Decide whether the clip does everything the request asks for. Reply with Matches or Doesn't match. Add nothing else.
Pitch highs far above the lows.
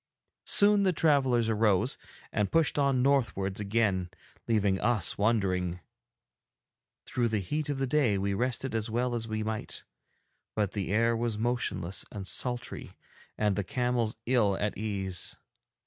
Doesn't match